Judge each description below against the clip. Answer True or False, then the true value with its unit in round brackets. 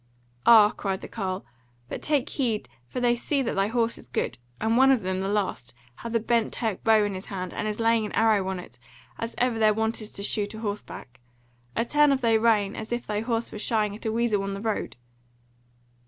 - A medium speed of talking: False (230 wpm)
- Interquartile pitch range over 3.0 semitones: False (2.4 semitones)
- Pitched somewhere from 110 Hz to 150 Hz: False (220 Hz)